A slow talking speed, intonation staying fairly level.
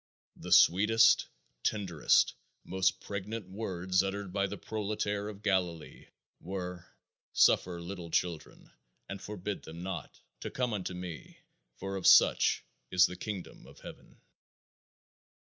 Yes: slow, 125 wpm; narrow, 2.3 semitones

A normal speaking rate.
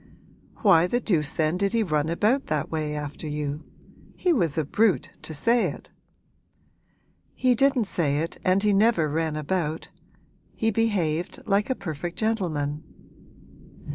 Yes: average, 145 wpm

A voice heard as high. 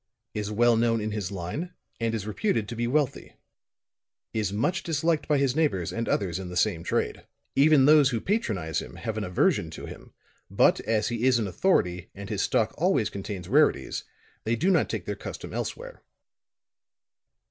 No: low, 115 Hz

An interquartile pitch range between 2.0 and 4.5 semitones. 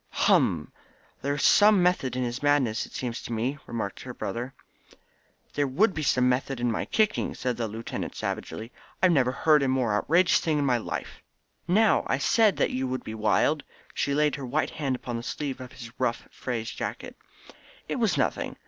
Yes: average, 3.8 semitones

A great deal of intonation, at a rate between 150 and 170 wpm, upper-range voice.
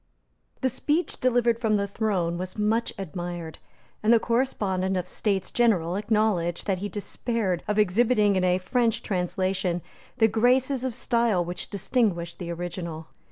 No: average, 4.4 semitones; average, 155 wpm; high, 200 Hz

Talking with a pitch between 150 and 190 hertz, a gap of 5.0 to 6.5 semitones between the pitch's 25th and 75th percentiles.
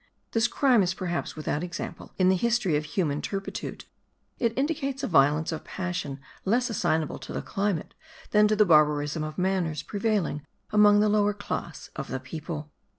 Yes: medium, 185 Hz; wide, 5.5 semitones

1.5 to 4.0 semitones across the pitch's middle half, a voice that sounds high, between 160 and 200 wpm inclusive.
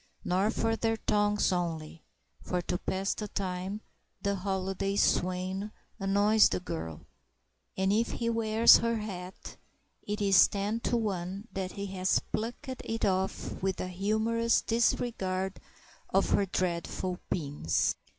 No: average, 2.8 semitones; high, 195 Hz; slow, 135 wpm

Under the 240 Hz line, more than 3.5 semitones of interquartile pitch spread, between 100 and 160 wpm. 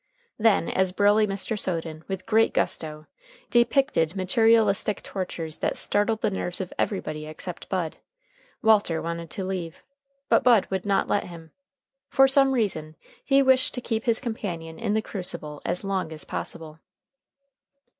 Yes: high, 190 Hz; average, 5.0 semitones; average, 150 wpm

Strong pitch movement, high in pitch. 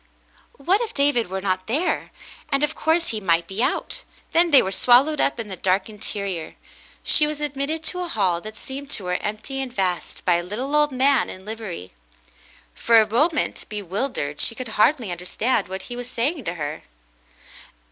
Yes: wide, 6.9 semitones; high, 230 Hz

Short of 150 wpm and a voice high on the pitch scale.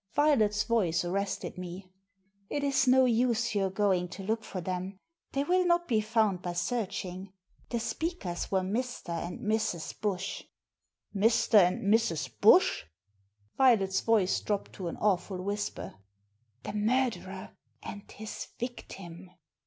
Yes: average, 140 wpm; high, 200 Hz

